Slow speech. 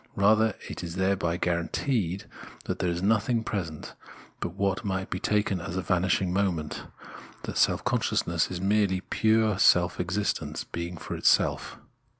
No: average, 155 wpm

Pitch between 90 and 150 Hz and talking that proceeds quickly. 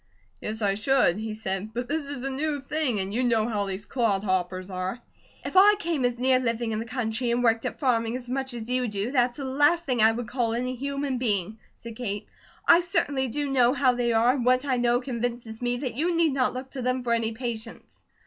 No: high, 245 Hz; fast, 235 wpm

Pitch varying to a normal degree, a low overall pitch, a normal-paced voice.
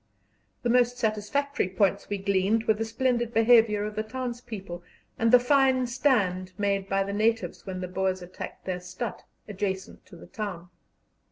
No: average, 3.9 semitones; high, 210 Hz; average, 165 wpm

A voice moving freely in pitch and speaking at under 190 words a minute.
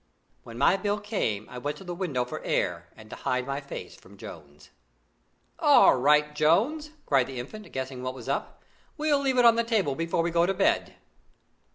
No: wide, 8.4 semitones; average, 200 wpm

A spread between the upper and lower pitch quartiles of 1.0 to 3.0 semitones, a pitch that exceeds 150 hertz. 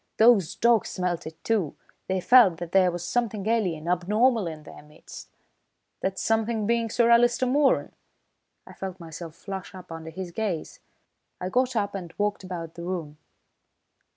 No: average, 4.8 semitones; high, 190 Hz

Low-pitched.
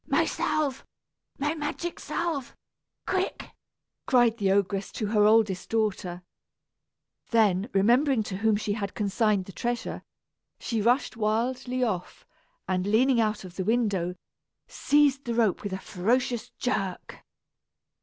No: high, 220 Hz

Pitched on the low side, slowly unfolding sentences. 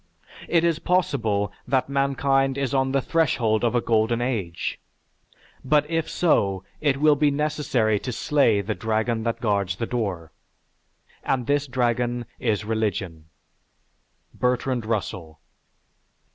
Yes: low, 120 Hz; slow, 130 wpm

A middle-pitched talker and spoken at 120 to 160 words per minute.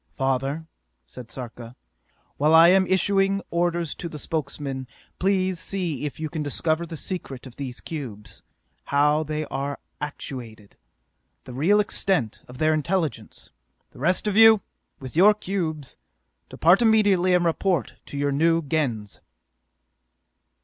Yes: medium, 155 Hz; slow, 135 wpm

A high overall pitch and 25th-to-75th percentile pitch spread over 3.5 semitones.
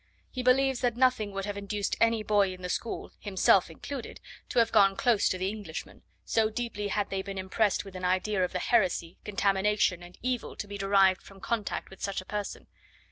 No: high, 200 Hz; average, 2.7 semitones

